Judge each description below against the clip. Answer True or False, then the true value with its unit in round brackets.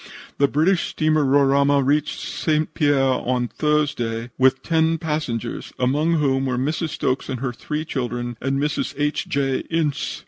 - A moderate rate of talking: True (150 wpm)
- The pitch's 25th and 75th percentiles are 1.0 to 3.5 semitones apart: True (2.8 semitones)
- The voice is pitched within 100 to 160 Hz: True (140 Hz)